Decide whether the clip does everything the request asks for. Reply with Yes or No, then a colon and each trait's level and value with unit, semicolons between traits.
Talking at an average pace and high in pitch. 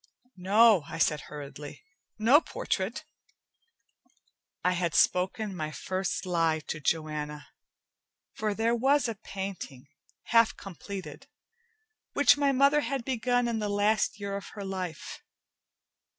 No: slow, 120 wpm; high, 200 Hz